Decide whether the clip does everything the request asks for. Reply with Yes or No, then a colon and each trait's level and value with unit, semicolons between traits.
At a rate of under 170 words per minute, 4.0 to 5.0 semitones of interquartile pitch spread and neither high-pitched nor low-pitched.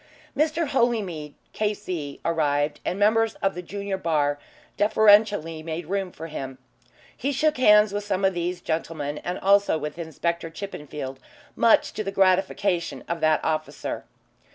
Yes: average, 145 wpm; average, 4.6 semitones; medium, 180 Hz